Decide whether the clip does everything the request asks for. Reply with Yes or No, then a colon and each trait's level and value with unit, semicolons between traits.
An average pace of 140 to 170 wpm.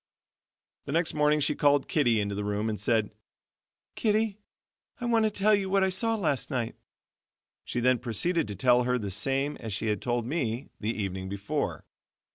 No: average, 185 wpm